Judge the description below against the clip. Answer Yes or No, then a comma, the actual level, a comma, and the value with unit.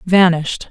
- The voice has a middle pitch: Yes, medium, 175 Hz